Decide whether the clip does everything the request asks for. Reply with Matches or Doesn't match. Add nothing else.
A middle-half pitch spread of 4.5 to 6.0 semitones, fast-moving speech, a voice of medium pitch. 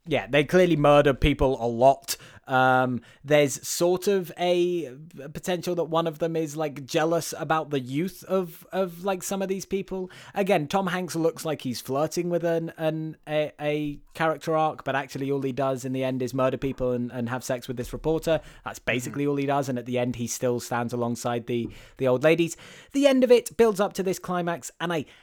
Matches